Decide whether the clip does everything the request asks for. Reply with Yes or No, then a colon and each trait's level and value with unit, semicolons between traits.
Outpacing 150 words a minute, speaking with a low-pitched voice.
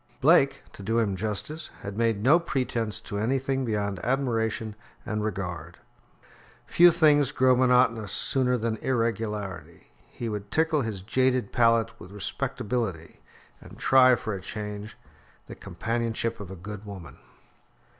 No: slow, 135 wpm; low, 115 Hz